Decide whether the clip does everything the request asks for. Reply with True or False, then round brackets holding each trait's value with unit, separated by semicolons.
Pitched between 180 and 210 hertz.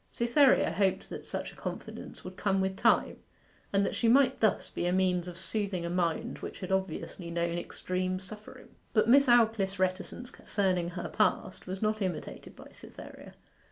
True (190 Hz)